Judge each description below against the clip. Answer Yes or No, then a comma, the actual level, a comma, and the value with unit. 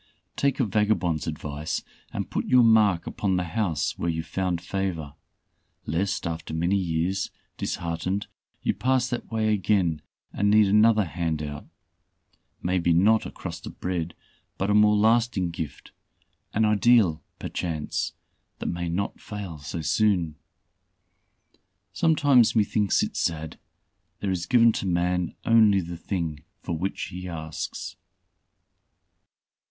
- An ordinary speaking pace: No, slow, 130 wpm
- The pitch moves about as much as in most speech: Yes, average, 4.2 semitones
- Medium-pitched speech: No, very low, 95 Hz